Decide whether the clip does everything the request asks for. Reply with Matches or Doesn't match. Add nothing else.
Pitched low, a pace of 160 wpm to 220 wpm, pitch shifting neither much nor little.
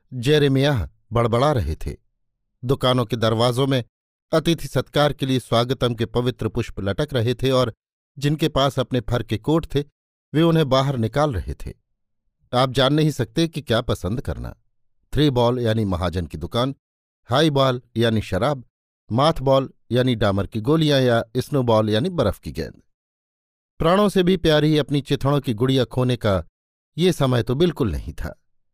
Matches